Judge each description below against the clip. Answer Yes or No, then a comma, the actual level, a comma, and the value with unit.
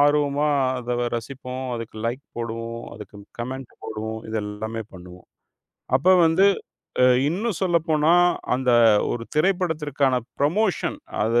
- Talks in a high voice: No, low, 130 Hz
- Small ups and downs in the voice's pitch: No, average, 5.0 semitones